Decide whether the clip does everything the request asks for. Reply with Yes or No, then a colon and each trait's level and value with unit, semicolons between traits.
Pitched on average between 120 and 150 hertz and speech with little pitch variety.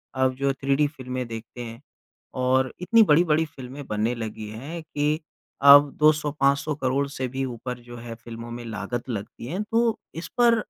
No: low, 135 Hz; average, 3.9 semitones